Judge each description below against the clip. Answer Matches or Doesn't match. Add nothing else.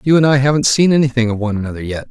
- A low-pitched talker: Matches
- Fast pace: Matches